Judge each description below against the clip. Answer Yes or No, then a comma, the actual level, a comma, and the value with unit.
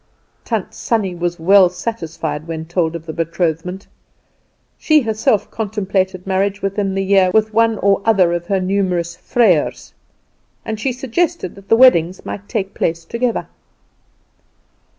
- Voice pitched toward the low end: No, high, 195 Hz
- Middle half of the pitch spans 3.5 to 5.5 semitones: Yes, average, 4.0 semitones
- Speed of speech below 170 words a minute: Yes, average, 140 wpm